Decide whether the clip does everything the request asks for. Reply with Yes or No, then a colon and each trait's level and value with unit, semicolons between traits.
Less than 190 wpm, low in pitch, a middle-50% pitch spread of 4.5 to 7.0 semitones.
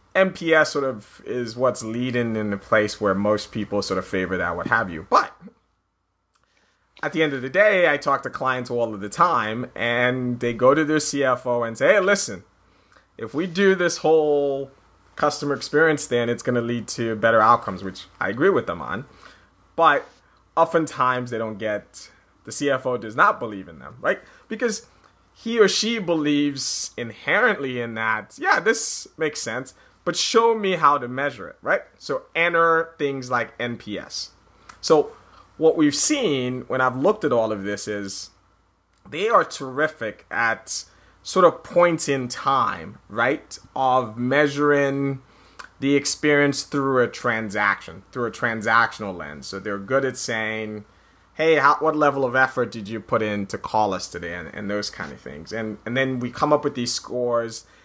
Yes: average, 175 wpm; low, 125 Hz; average, 5.2 semitones